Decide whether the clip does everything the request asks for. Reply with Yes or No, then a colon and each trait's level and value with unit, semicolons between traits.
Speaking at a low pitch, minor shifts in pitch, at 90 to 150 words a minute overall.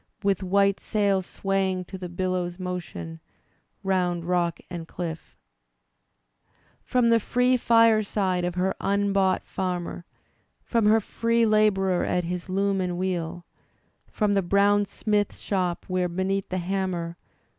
No: high, 190 Hz; narrow, 2.2 semitones; average, 140 wpm